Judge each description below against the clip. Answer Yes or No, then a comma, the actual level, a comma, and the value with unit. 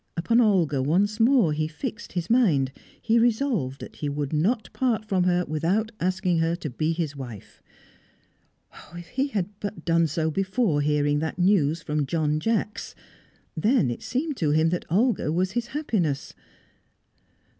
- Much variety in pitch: Yes, wide, 6.2 semitones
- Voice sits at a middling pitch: Yes, medium, 175 Hz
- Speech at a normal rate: Yes, average, 160 wpm